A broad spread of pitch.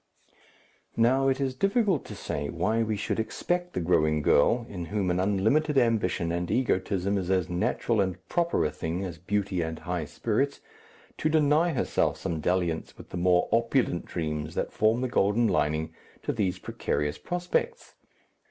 Yes: wide, 6.8 semitones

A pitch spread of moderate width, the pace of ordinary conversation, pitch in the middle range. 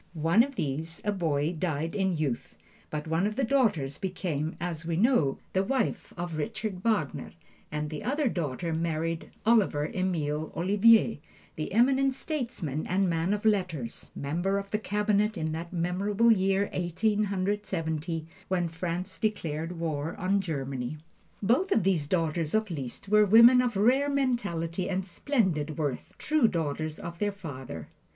Yes: average, 4.9 semitones; average, 155 wpm; medium, 180 Hz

